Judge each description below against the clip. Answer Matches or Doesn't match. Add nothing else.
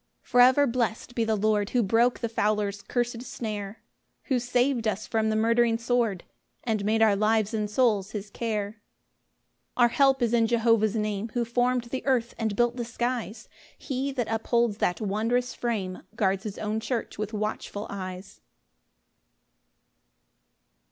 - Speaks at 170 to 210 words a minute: Doesn't match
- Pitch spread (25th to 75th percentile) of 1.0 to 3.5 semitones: Matches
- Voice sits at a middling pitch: Doesn't match